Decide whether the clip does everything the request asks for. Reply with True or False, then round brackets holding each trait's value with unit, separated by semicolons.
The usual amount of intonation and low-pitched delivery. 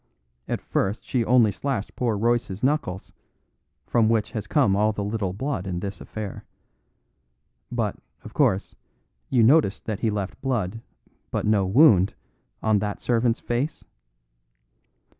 True (3.3 semitones; 110 Hz)